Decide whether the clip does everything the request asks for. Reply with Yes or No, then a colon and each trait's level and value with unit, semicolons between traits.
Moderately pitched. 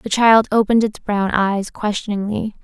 No: high, 210 Hz